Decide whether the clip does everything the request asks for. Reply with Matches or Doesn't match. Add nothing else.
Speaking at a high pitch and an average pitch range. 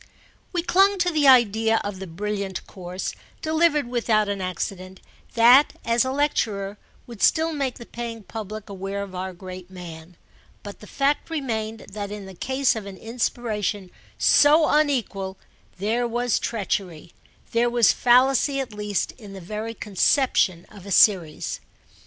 Matches